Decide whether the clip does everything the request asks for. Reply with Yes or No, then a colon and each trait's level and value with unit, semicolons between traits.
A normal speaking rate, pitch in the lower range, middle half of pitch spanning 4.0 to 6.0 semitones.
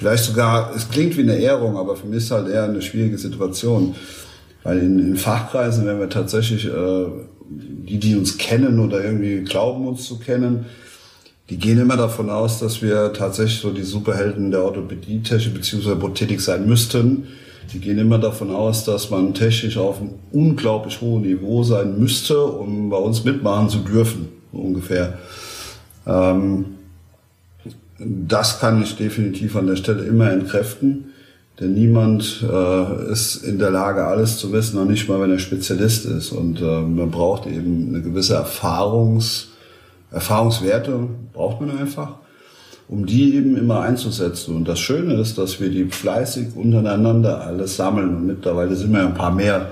No: average, 165 wpm; low, 105 Hz; average, 3.3 semitones